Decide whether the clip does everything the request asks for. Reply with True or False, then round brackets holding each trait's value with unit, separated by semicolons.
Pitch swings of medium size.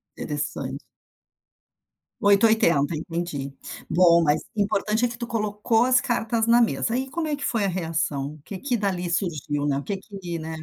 False (5.9 semitones)